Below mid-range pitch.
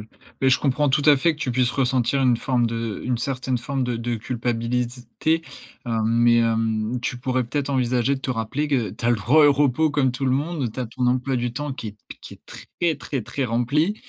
Yes: low, 125 Hz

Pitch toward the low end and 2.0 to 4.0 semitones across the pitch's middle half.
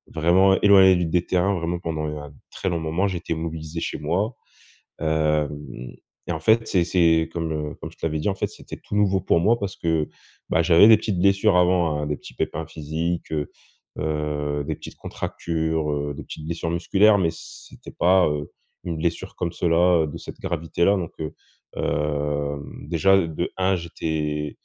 Yes: very low, 85 Hz; average, 2.9 semitones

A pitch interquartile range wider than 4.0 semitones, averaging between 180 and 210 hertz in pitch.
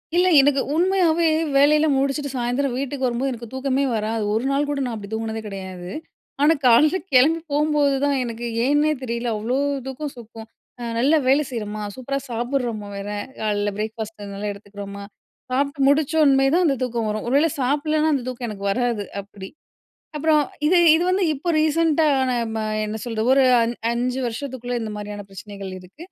No: average, 4.7 semitones; very high, 250 Hz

